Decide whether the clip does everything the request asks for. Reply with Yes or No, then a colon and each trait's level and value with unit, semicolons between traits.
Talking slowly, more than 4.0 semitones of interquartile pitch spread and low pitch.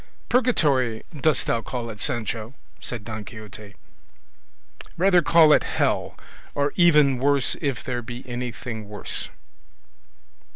Yes: slow, 120 wpm; average, 4.7 semitones; low, 125 Hz